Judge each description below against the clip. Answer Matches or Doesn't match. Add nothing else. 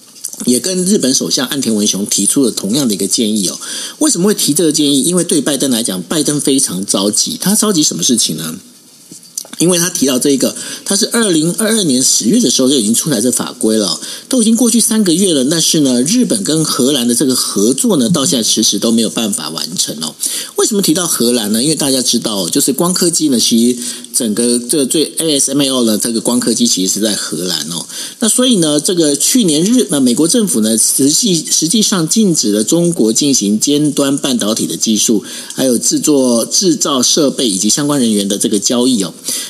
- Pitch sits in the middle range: Matches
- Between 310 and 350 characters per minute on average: Matches